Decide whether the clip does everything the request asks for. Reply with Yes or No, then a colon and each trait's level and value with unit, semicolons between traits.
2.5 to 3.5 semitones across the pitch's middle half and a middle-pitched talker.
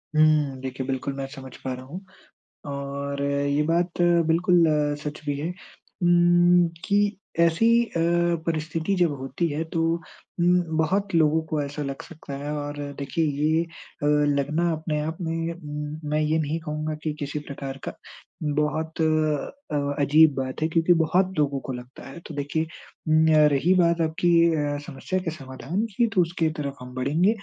Yes: average, 3.0 semitones; medium, 155 Hz